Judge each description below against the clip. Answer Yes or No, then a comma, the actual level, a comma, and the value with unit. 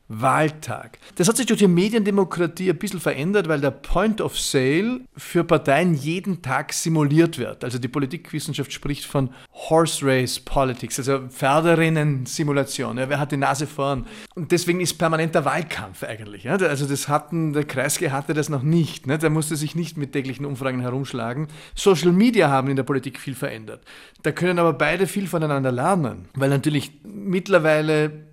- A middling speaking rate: Yes, average, 170 wpm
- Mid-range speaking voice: Yes, medium, 150 Hz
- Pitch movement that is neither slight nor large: Yes, average, 3.8 semitones